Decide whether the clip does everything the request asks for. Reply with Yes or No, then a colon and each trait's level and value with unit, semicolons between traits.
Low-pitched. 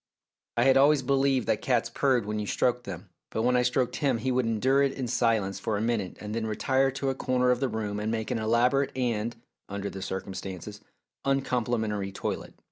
Yes: low, 120 Hz